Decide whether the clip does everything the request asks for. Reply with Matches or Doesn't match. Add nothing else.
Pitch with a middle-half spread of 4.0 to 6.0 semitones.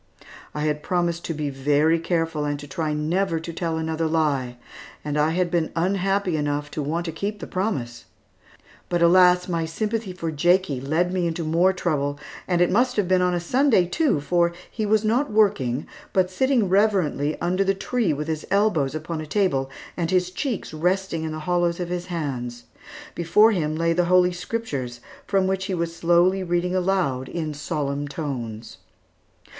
Doesn't match